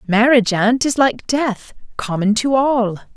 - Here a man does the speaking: No, female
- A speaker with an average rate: Yes, average, 150 wpm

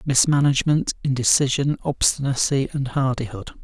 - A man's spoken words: Yes, male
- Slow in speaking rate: Yes, slow, 85 wpm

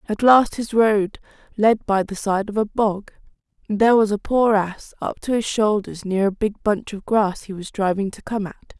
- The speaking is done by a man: No, female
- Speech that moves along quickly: Yes, fast, 225 wpm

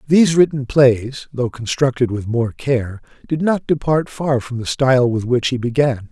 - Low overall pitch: Yes, low, 130 Hz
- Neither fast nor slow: Yes, average, 185 wpm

